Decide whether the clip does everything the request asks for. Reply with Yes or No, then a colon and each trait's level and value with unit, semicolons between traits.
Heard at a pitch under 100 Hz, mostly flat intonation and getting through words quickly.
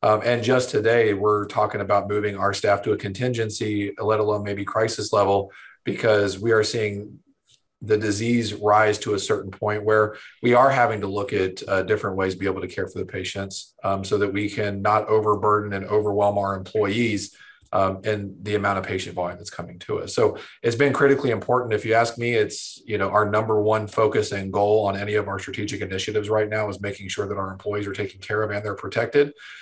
No: low, 105 Hz; narrow, 1.4 semitones; fast, 220 wpm